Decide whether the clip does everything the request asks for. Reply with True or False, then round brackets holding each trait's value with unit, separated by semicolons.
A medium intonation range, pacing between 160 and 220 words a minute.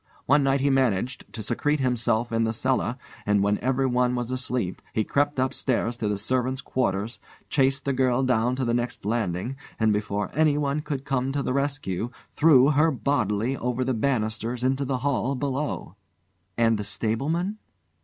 True (3.3 semitones; 170 wpm)